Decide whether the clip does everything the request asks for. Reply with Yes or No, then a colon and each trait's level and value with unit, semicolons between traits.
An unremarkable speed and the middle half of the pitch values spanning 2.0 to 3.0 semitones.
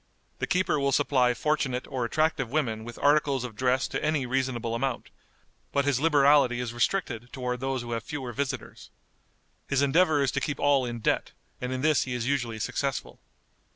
Yes: average, 185 wpm; average, 2.7 semitones